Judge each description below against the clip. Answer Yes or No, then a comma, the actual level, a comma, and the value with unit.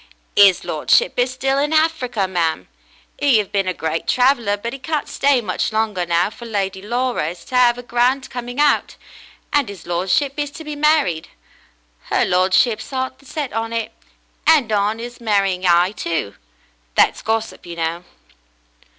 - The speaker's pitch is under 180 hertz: No, high, 225 Hz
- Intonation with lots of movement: Yes, wide, 5.8 semitones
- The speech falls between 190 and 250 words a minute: No, average, 170 wpm